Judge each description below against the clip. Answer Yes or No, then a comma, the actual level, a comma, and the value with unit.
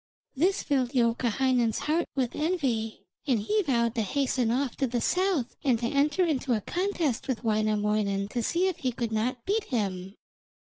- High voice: Yes, very high, 250 Hz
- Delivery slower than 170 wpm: No, average, 175 wpm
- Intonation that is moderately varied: Yes, average, 4.8 semitones